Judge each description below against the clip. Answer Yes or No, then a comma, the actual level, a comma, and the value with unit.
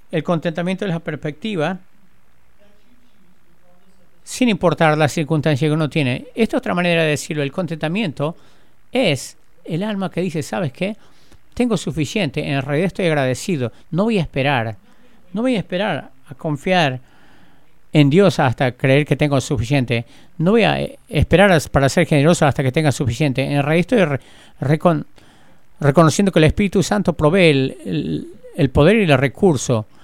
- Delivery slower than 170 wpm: Yes, average, 160 wpm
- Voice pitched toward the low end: No, medium, 155 Hz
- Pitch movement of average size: Yes, average, 4.3 semitones